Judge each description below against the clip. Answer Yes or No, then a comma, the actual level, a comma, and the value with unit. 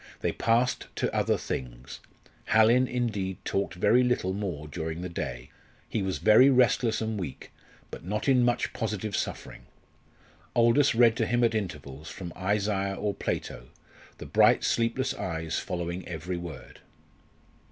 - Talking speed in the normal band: Yes, average, 145 wpm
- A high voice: No, low, 100 Hz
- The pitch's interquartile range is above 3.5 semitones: Yes, average, 5.1 semitones